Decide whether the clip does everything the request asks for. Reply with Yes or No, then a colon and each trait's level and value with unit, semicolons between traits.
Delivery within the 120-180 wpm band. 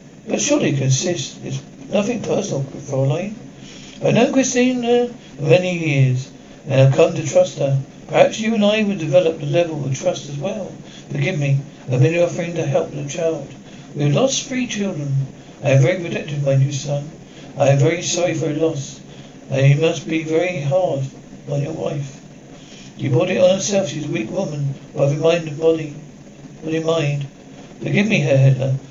No: average, 195 wpm